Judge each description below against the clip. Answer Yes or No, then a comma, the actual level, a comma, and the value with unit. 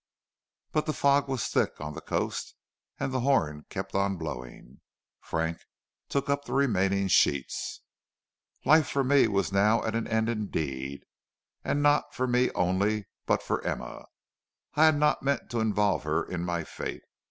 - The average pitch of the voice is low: Yes, low, 105 Hz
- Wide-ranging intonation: Yes, wide, 8.1 semitones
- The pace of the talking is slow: No, average, 165 wpm